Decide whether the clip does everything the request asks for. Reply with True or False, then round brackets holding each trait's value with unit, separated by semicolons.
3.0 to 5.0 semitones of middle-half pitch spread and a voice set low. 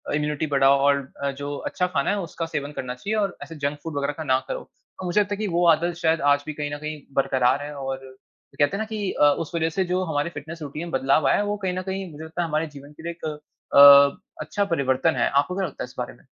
False (3.4 semitones; 150 Hz)